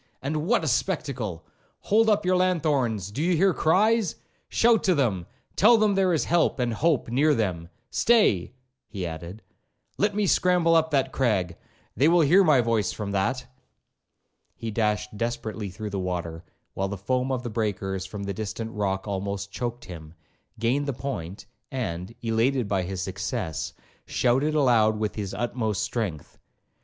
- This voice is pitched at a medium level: No, low, 115 Hz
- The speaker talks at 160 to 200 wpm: No, average, 150 wpm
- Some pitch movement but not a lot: No, wide, 7.6 semitones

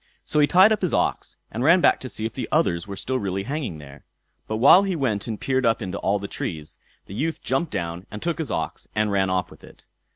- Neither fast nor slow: No, fast, 255 wpm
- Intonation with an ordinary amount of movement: No, wide, 7.6 semitones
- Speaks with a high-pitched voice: No, low, 110 Hz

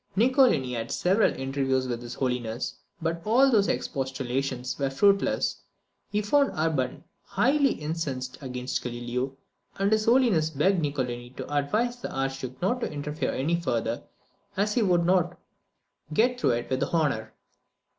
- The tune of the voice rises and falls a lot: Yes, wide, 7.7 semitones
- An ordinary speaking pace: Yes, average, 145 wpm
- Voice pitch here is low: No, medium, 145 Hz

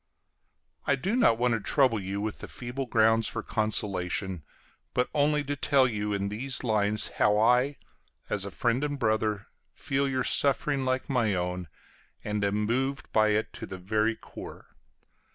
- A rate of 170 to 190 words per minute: No, average, 160 wpm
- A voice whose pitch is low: Yes, low, 115 Hz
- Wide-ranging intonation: No, average, 4.2 semitones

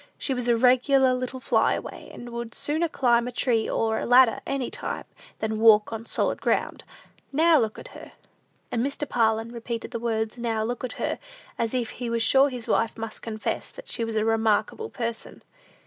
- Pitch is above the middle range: Yes, high, 235 Hz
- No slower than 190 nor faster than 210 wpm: Yes, average, 195 wpm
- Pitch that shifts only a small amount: Yes, narrow, 2.2 semitones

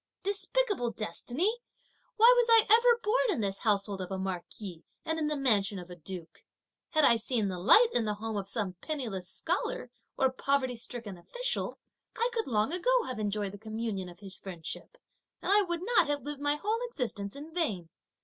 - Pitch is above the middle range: Yes, high, 240 Hz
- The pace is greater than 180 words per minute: Yes, average, 190 wpm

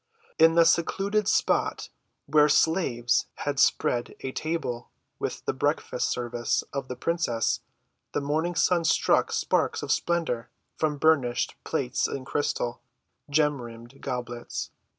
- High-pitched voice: No, medium, 140 Hz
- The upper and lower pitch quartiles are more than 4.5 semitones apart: Yes, average, 5.1 semitones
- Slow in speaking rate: Yes, slow, 125 wpm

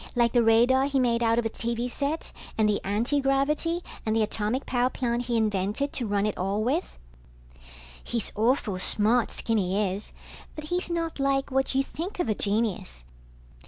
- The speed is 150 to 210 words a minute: Yes, average, 175 wpm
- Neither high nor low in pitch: No, high, 235 Hz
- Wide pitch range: No, average, 4.3 semitones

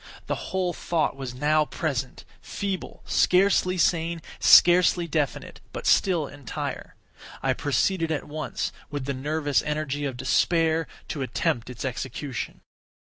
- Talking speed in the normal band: No, slow, 120 wpm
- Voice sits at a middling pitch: Yes, medium, 150 Hz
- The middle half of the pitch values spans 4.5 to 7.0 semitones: No, average, 3.7 semitones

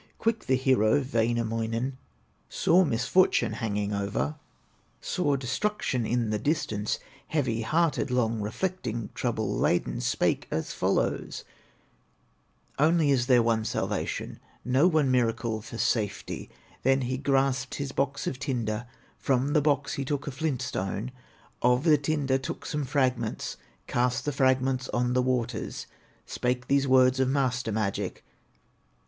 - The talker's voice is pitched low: Yes, low, 130 Hz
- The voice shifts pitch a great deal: No, average, 3.3 semitones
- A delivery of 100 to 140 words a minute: Yes, slow, 135 wpm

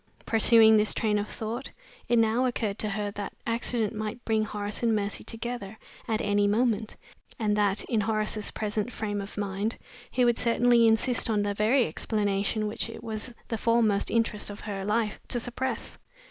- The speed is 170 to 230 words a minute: Yes, average, 175 wpm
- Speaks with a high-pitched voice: Yes, high, 215 Hz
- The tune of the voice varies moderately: No, narrow, 1.9 semitones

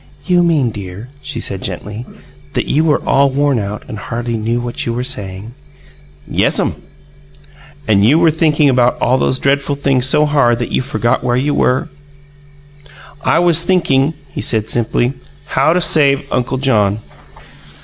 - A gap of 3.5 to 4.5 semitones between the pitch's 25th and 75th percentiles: Yes, average, 4.0 semitones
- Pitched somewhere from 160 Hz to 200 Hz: No, low, 130 Hz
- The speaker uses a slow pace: No, average, 160 wpm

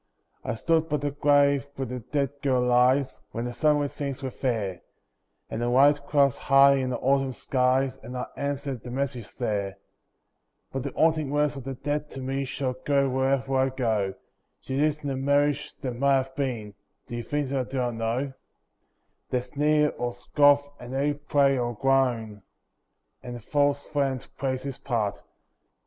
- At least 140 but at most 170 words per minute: No, average, 180 wpm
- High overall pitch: No, low, 135 Hz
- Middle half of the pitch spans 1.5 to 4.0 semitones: Yes, narrow, 2.4 semitones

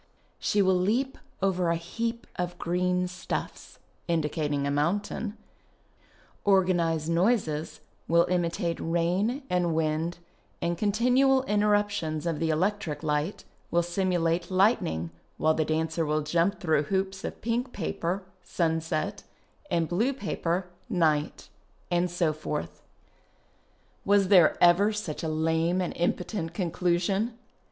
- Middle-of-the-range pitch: Yes, medium, 175 Hz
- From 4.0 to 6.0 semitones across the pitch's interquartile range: No, average, 3.5 semitones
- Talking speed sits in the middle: No, slow, 130 wpm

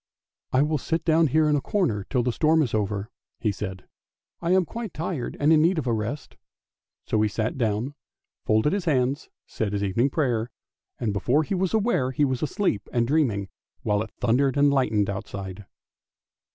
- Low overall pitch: Yes, low, 130 Hz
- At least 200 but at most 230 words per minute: Yes, fast, 205 wpm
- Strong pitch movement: Yes, wide, 6.4 semitones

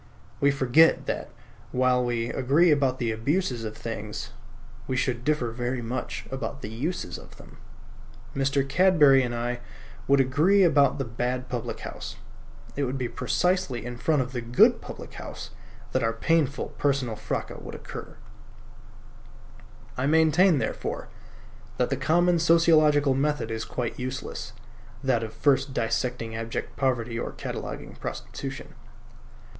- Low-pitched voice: Yes, low, 130 Hz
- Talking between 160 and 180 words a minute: No, average, 140 wpm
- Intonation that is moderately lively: Yes, average, 3.5 semitones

